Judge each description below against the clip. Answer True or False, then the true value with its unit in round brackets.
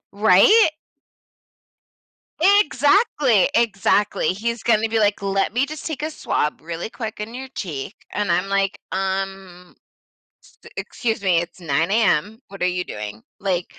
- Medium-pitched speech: False (200 Hz)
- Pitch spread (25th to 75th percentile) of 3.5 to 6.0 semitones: True (4.4 semitones)